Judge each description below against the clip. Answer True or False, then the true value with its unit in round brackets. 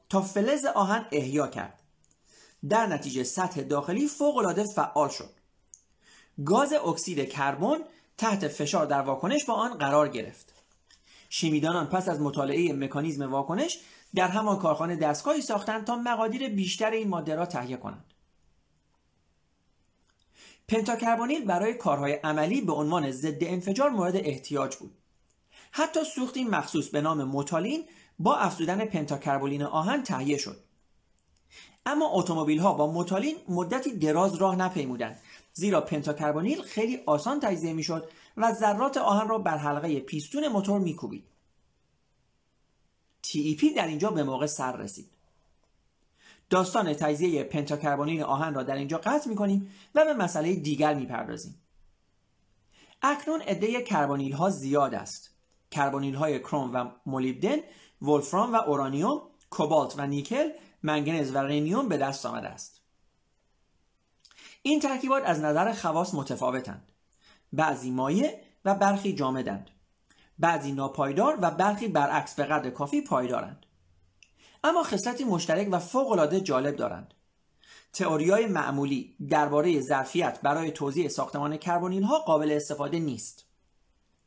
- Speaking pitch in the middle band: True (155 Hz)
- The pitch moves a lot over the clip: True (6.7 semitones)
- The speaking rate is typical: True (125 wpm)